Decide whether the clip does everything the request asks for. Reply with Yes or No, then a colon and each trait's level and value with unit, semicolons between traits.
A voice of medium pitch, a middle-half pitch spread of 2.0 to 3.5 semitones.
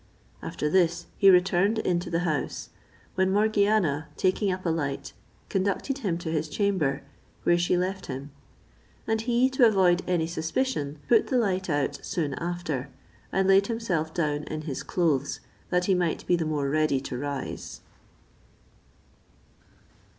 No: medium, 175 Hz; average, 4.0 semitones